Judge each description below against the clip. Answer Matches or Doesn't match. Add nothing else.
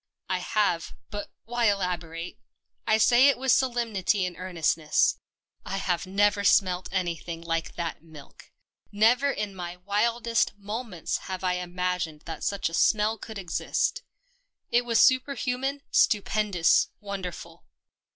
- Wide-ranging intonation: Doesn't match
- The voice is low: Doesn't match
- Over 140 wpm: Doesn't match